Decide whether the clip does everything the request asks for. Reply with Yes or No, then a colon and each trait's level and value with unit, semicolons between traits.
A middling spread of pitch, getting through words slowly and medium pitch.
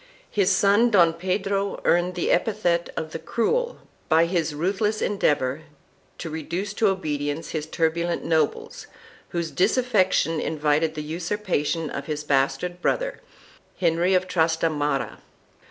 Yes: average, 3.7 semitones; slow, 130 wpm; medium, 170 Hz